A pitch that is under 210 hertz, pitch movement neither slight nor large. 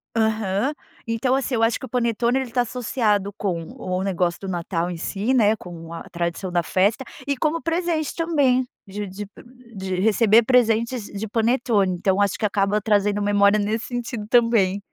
No: high, 215 Hz; average, 3.9 semitones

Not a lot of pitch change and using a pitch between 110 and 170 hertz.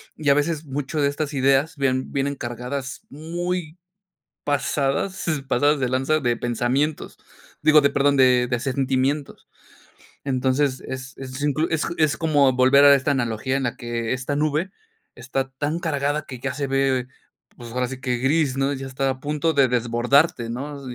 Yes: narrow, 2.2 semitones; low, 135 Hz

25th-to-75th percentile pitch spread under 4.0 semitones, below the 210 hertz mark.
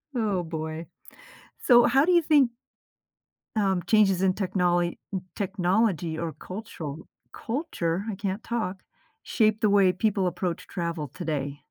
No: average, 4.3 semitones; high, 190 Hz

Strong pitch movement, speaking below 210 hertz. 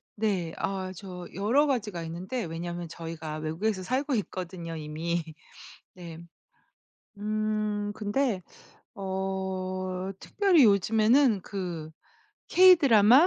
No: average, 3.9 semitones; high, 190 Hz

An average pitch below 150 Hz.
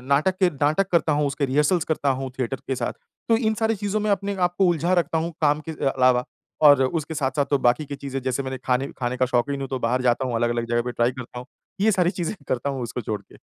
Yes: medium, 140 Hz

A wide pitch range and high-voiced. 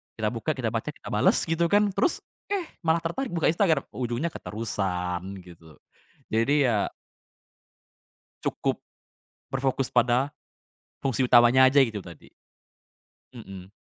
No: wide, 7.8 semitones; low, 125 Hz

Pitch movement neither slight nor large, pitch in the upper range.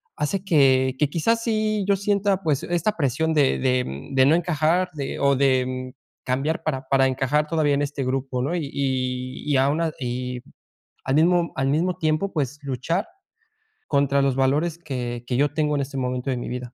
No: average, 3.7 semitones; medium, 140 Hz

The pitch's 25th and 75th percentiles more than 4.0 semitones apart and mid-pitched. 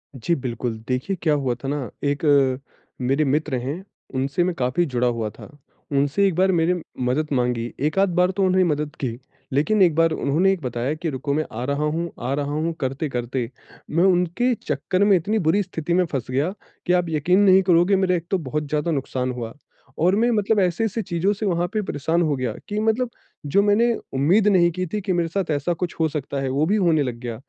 Yes: average, 5.2 semitones; medium, 160 Hz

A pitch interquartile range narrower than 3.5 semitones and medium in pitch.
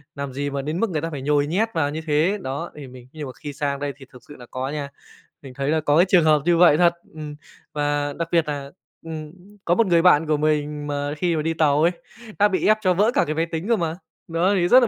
Yes: average, 2.9 semitones; medium, 155 Hz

